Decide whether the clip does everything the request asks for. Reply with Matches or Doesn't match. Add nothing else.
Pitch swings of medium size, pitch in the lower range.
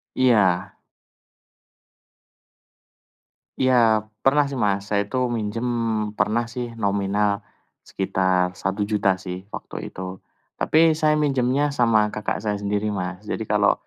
Matches